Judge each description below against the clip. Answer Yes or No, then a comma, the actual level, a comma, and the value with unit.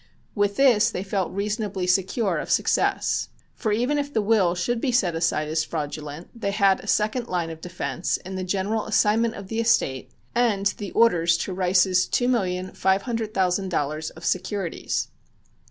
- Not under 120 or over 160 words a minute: No, average, 175 wpm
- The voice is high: Yes, high, 195 Hz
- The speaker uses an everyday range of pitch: Yes, average, 3.8 semitones